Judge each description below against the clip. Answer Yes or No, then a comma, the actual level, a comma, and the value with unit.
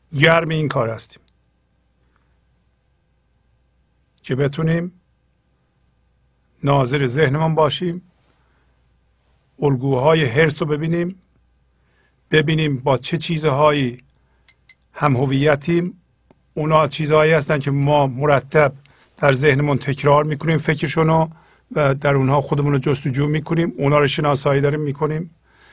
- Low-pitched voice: No, medium, 145 Hz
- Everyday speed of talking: No, slow, 100 wpm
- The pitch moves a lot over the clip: No, average, 3.3 semitones